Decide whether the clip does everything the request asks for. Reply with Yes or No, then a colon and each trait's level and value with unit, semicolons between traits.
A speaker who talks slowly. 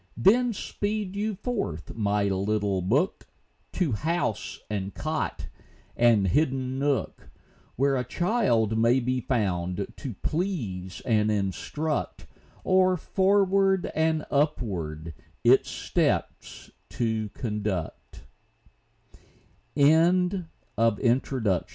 Yes: slow, 90 wpm